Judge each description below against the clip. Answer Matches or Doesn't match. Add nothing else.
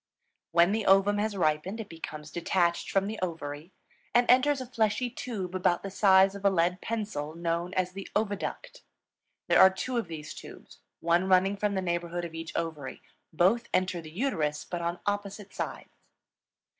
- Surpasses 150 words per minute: Matches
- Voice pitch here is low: Doesn't match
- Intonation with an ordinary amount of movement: Matches